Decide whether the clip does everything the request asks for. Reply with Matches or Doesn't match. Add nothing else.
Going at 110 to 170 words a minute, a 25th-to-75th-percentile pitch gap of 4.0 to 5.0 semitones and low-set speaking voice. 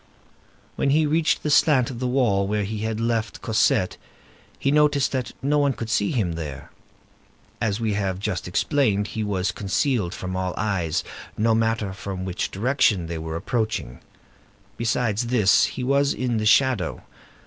Matches